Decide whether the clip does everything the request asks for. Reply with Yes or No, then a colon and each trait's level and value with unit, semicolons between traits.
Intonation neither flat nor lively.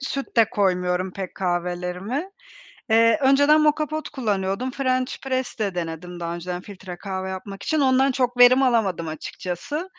No: wide, 6.7 semitones